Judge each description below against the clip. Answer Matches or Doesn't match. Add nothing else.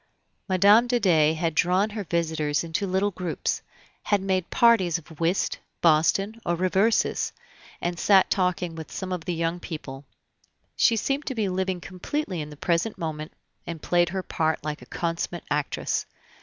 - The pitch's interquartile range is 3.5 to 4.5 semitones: Doesn't match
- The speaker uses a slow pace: Doesn't match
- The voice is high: Doesn't match